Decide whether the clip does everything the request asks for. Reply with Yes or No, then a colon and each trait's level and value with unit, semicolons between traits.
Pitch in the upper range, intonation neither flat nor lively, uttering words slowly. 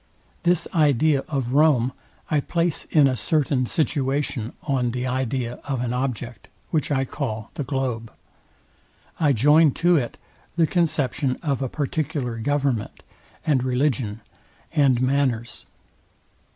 No: low, 135 Hz; average, 3.1 semitones; slow, 125 wpm